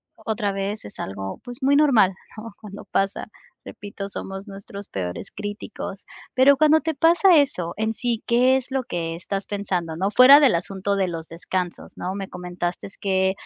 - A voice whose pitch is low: No, high, 200 Hz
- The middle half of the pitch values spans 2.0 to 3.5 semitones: No, average, 4.9 semitones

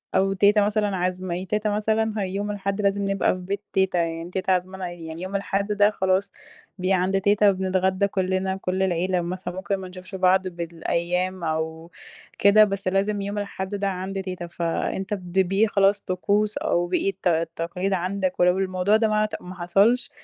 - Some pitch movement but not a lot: No, narrow, 1.7 semitones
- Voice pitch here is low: No, high, 190 Hz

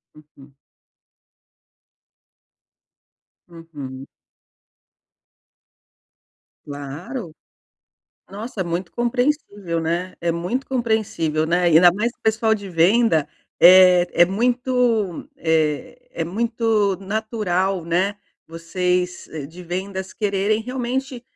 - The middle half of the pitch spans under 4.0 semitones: No, average, 5.1 semitones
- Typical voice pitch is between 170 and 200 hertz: Yes, high, 190 Hz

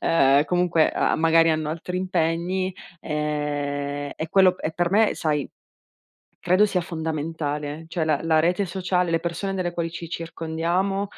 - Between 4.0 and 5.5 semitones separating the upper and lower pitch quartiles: No, narrow, 2.5 semitones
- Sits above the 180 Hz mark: No, medium, 165 Hz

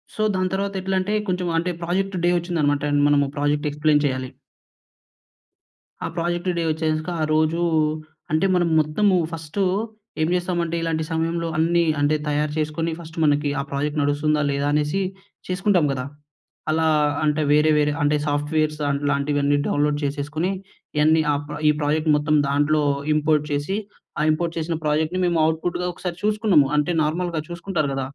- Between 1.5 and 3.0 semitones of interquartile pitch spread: Yes, average, 2.7 semitones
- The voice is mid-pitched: Yes, medium, 155 Hz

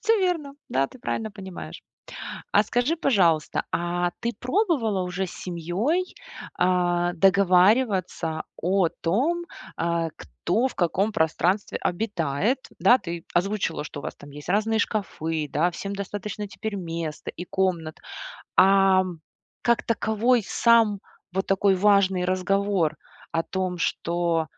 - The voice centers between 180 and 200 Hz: Yes, high, 190 Hz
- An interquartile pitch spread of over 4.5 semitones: No, average, 3.9 semitones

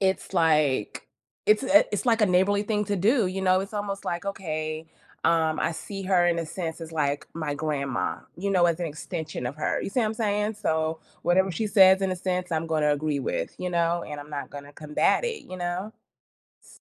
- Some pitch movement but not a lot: Yes, average, 4.0 semitones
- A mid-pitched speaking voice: Yes, medium, 175 Hz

